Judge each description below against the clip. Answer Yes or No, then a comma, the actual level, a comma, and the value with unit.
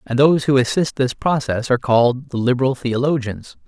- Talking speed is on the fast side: No, average, 180 wpm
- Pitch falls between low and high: No, low, 130 Hz